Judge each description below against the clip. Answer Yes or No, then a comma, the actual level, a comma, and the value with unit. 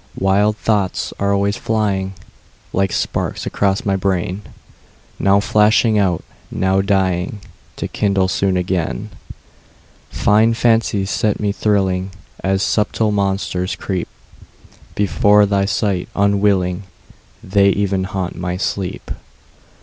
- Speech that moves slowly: Yes, slow, 90 wpm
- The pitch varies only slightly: Yes, narrow, 1.5 semitones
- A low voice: Yes, low, 100 Hz